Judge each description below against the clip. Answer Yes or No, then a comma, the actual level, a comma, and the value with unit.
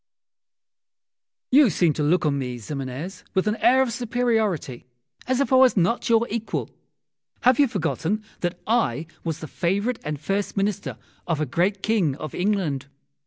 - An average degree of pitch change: No, wide, 6.9 semitones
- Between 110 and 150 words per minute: No, average, 165 wpm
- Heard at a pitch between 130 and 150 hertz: No, high, 190 Hz